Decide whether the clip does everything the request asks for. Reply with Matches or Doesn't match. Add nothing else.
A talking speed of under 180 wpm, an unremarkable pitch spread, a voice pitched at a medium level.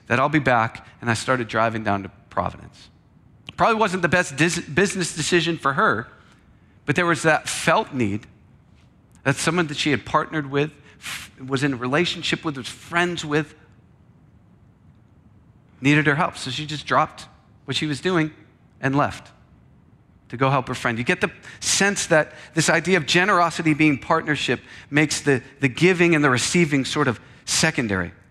Matches